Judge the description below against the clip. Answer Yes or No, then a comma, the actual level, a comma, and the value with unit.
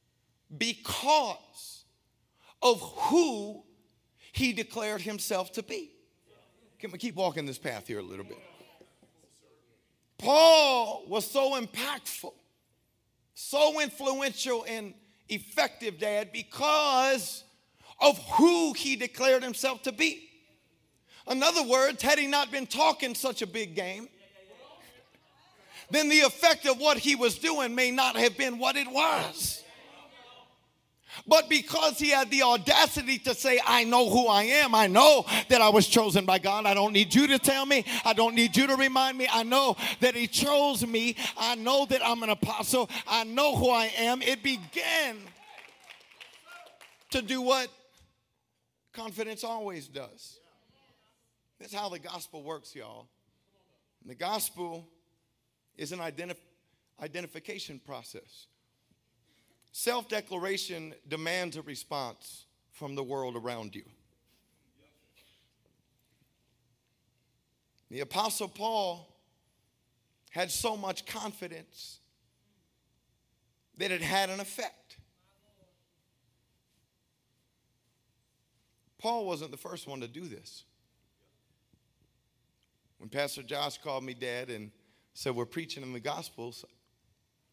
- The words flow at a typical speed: No, slow, 125 wpm